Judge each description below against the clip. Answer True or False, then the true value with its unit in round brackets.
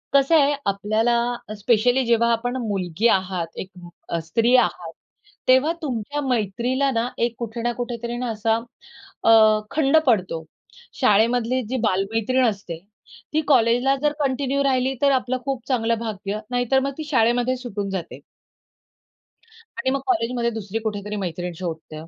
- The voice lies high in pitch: True (235 Hz)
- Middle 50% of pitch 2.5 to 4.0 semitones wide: True (3.6 semitones)